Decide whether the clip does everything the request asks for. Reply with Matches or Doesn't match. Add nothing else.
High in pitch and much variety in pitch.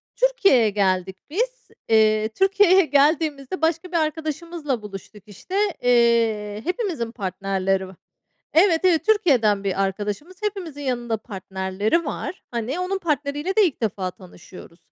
Matches